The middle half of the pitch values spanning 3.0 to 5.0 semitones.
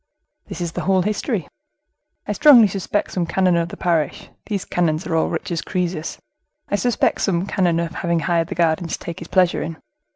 No: narrow, 2.6 semitones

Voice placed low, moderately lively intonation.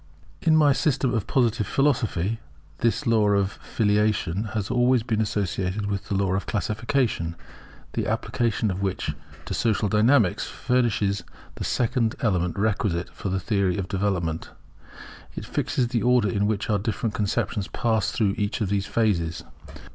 Yes: low, 105 Hz; average, 3.0 semitones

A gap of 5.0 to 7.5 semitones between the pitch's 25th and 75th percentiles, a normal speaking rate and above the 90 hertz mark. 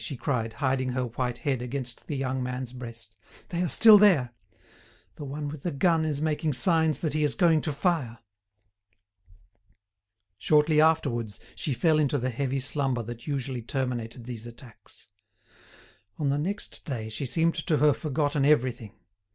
No: average, 3.8 semitones; average, 160 wpm; low, 135 Hz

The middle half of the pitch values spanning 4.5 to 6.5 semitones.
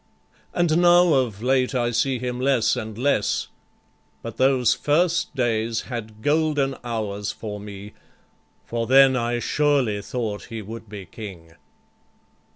No: average, 3.9 semitones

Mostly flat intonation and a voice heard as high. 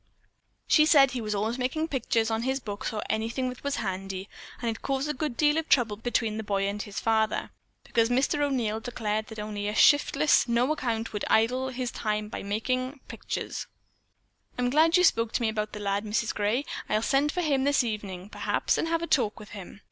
No: average, 4.2 semitones; high, 230 Hz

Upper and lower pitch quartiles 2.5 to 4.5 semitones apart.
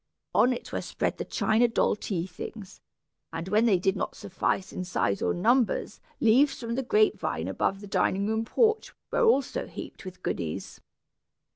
No: average, 5.2 semitones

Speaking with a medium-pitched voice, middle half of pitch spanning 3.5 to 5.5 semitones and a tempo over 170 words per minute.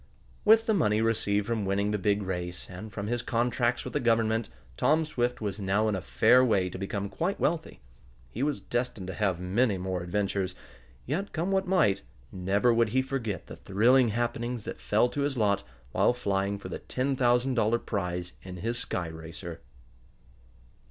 No: low, 110 Hz; average, 4.3 semitones; average, 185 wpm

